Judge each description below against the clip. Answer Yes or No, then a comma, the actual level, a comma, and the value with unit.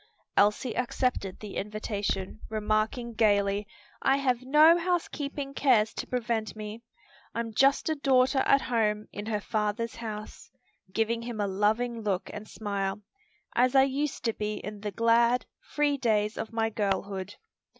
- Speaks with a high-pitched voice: Yes, high, 225 Hz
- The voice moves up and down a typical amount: Yes, average, 3.3 semitones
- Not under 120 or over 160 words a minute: Yes, average, 150 wpm